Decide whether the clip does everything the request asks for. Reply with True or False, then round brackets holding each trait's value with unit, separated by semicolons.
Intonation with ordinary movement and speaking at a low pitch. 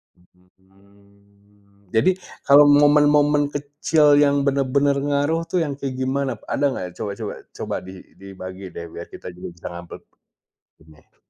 False (6.9 semitones; 110 Hz)